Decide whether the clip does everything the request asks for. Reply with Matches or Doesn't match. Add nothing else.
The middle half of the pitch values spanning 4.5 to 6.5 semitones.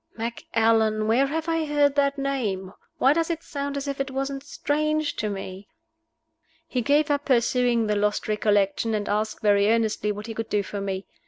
Matches